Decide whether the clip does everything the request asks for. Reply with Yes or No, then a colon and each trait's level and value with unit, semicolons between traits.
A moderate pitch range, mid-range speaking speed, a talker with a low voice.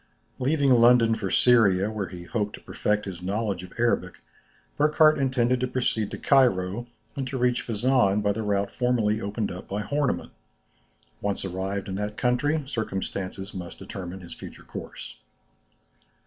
Yes: average, 4.3 semitones; average, 155 wpm; low, 105 Hz